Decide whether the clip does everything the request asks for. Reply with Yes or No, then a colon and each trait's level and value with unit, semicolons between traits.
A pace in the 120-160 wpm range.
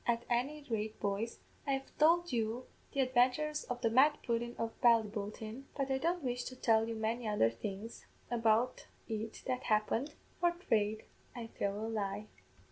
No: average, 170 wpm